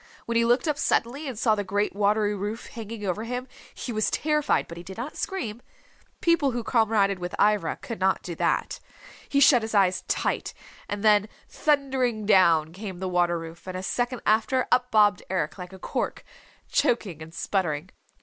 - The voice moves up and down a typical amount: Yes, average, 4.5 semitones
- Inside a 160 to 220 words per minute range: Yes, average, 190 wpm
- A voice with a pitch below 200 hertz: No, high, 210 Hz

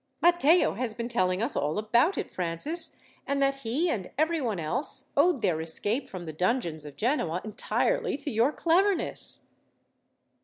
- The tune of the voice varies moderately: No, wide, 8.7 semitones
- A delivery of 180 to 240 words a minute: No, average, 155 wpm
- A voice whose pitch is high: Yes, high, 240 Hz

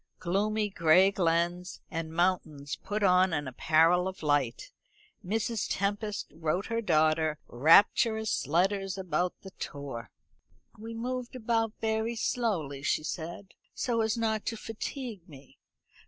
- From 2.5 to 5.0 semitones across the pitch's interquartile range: No, wide, 5.5 semitones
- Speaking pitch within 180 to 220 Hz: Yes, medium, 185 Hz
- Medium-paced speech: No, slow, 125 wpm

